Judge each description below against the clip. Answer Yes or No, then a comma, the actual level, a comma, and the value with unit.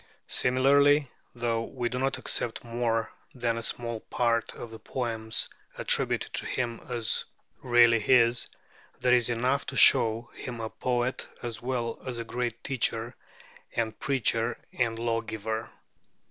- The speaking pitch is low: Yes, low, 120 Hz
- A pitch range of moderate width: No, narrow, 1.6 semitones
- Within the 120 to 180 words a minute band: Yes, average, 140 wpm